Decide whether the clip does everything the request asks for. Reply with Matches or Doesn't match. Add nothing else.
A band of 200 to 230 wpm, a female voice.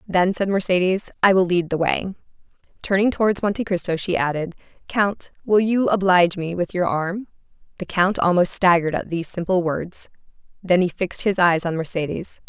Doesn't match